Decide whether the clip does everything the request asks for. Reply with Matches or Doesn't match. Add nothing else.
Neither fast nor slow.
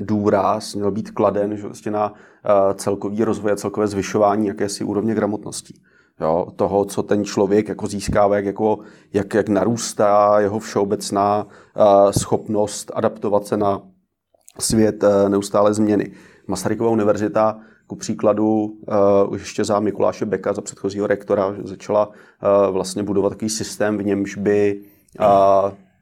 Matches